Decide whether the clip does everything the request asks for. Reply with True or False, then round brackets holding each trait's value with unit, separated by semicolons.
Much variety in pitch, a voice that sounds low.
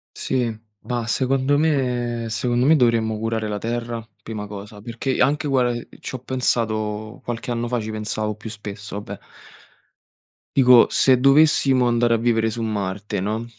False (2.6 semitones; 115 Hz)